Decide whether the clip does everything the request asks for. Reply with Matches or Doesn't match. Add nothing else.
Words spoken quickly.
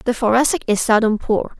Doesn't match